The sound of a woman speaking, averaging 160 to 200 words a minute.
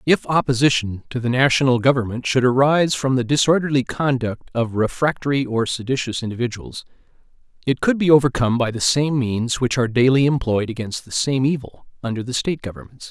No: male; average, 170 wpm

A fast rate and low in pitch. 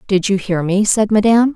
No: fast, 230 wpm; high, 205 Hz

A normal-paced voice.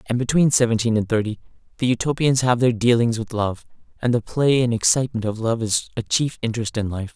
No: fast, 210 wpm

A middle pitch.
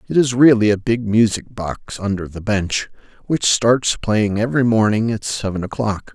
No: low, 110 Hz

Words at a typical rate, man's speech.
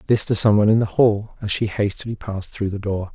No: fast, 265 wpm; male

